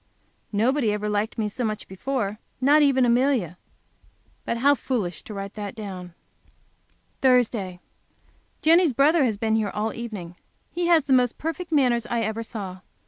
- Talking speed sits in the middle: Yes, average, 155 wpm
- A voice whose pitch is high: Yes, high, 230 Hz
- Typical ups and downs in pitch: Yes, average, 4.5 semitones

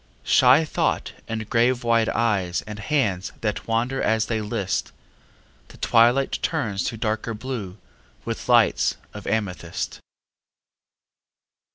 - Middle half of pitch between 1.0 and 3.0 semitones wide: Yes, narrow, 2.6 semitones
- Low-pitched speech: Yes, low, 115 Hz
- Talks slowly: Yes, slow, 115 wpm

